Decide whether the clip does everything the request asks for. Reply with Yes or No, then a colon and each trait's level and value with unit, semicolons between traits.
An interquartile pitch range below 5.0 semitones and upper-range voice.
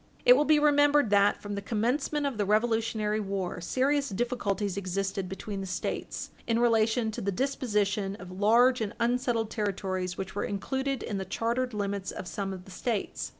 Yes: average, 3.8 semitones; high, 215 Hz